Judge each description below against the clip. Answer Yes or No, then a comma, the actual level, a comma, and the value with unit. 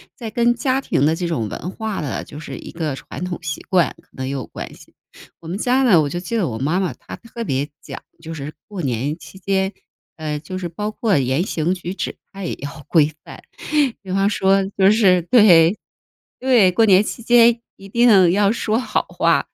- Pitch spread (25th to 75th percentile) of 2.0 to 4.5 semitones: No, wide, 5.4 semitones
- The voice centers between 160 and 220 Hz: Yes, medium, 185 Hz